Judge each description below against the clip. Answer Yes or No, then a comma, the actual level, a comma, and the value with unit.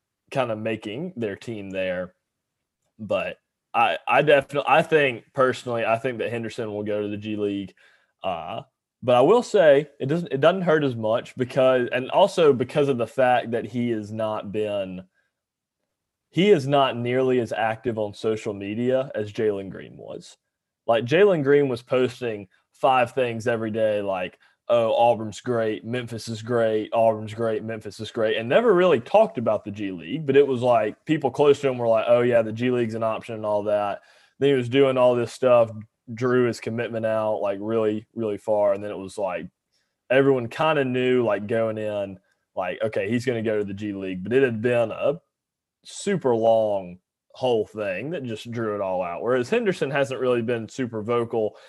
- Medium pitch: No, low, 115 Hz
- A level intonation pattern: No, average, 3.2 semitones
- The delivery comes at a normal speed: Yes, average, 195 wpm